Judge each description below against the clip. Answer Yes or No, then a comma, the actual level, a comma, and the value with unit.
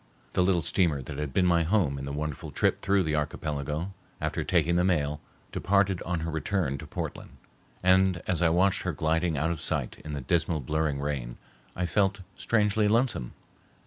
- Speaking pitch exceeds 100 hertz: No, very low, 85 Hz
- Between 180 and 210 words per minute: Yes, average, 185 wpm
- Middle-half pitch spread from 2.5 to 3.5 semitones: No, average, 4.1 semitones